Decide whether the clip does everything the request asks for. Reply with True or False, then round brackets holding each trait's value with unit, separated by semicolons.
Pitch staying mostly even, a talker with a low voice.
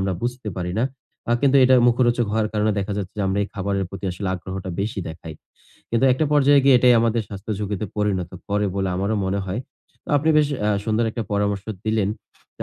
False (3.5 semitones; 105 Hz)